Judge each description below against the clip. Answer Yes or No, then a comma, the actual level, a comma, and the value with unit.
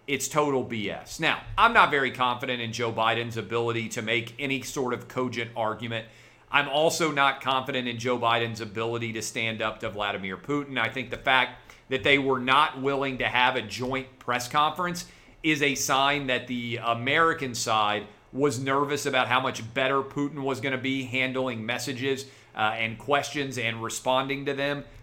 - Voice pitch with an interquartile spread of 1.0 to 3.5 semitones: Yes, average, 3.1 semitones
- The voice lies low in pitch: Yes, low, 125 Hz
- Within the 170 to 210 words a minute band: Yes, average, 180 wpm